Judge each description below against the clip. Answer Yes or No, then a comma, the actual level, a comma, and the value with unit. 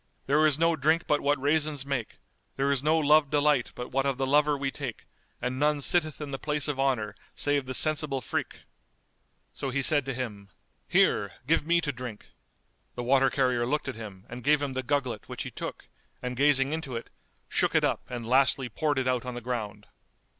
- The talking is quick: Yes, fast, 210 wpm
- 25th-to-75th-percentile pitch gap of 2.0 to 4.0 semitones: Yes, average, 2.9 semitones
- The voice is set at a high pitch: No, low, 135 Hz